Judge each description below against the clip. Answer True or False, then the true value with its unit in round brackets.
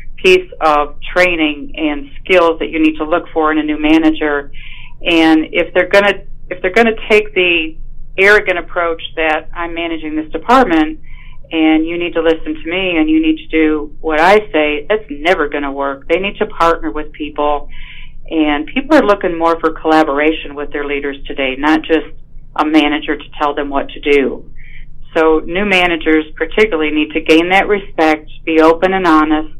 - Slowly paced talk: False (180 wpm)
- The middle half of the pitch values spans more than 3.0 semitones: False (2.7 semitones)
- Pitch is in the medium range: True (155 Hz)